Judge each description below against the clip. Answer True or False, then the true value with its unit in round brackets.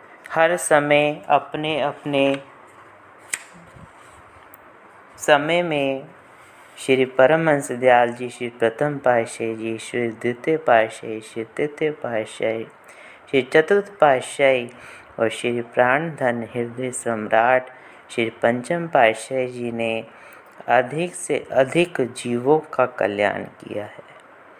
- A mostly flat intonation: False (4.0 semitones)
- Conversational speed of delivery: False (100 wpm)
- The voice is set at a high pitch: False (130 Hz)